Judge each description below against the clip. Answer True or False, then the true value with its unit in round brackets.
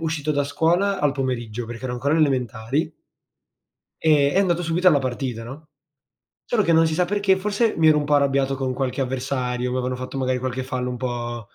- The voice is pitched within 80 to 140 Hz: True (135 Hz)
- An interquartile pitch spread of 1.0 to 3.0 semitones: False (4.2 semitones)